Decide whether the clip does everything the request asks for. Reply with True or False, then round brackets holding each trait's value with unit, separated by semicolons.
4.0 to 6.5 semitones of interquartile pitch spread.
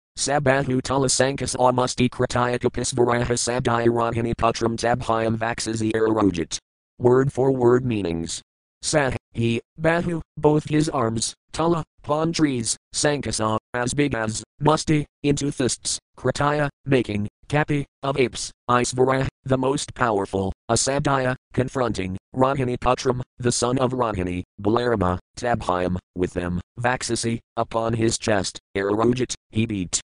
False (3.0 semitones)